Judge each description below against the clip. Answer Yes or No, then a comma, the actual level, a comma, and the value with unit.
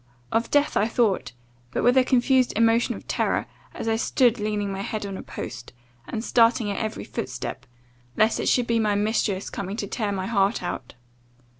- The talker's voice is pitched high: Yes, high, 220 Hz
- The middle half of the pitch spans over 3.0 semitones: No, average, 2.7 semitones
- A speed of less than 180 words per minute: No, average, 190 wpm